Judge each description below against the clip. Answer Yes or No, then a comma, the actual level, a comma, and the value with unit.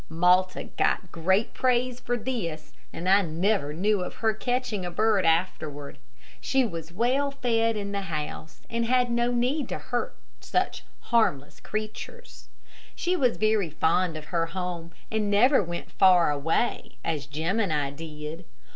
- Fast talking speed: No, average, 155 wpm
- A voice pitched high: Yes, high, 195 Hz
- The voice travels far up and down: Yes, wide, 6.3 semitones